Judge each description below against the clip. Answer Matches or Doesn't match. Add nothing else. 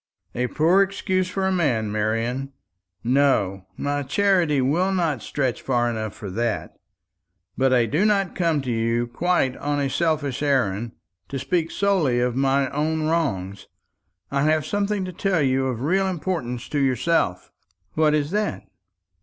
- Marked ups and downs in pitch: Matches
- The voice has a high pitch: Doesn't match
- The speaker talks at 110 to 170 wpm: Matches